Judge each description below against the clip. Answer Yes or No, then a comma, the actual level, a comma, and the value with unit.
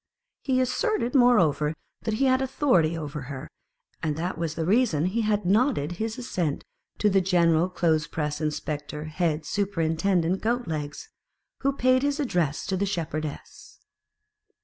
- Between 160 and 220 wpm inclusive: No, average, 150 wpm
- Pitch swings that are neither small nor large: No, wide, 7.1 semitones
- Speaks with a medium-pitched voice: Yes, medium, 180 Hz